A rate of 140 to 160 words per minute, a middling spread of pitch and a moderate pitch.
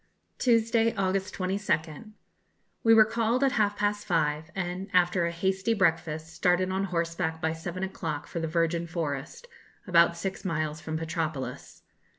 Yes: average, 150 wpm; average, 3.3 semitones; medium, 175 Hz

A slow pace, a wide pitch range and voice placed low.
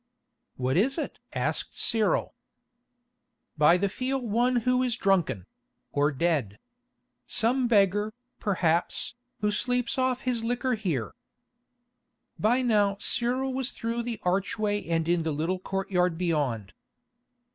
No: slow, 120 wpm; wide, 6.2 semitones; high, 205 Hz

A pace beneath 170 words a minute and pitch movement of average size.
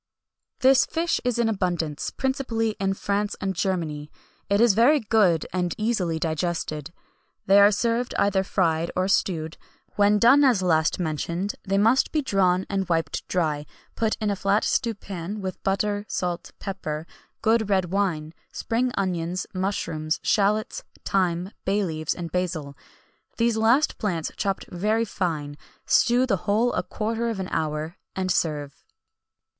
Yes: average, 150 wpm; average, 4.4 semitones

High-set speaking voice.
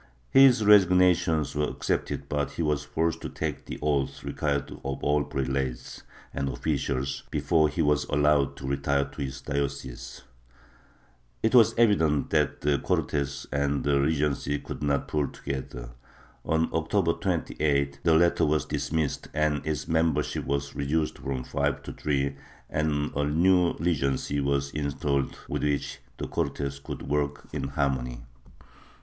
No: very low, 75 Hz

